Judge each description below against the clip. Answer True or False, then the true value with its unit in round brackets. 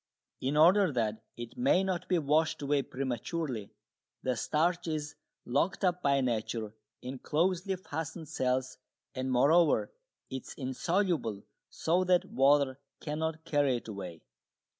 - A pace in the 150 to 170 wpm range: False (135 wpm)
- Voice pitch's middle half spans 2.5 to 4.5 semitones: False (4.9 semitones)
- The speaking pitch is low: False (145 Hz)